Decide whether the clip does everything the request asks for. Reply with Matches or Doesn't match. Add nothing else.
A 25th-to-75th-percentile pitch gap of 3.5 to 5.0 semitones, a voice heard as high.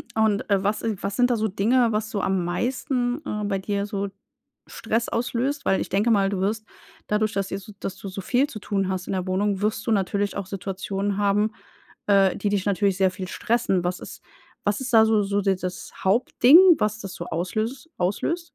Doesn't match